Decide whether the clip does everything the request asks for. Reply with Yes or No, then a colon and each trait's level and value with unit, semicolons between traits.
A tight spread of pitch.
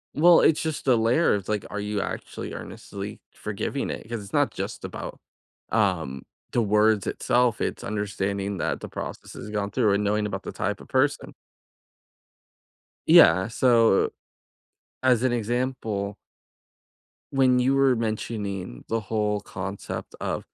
No: average, 3.5 semitones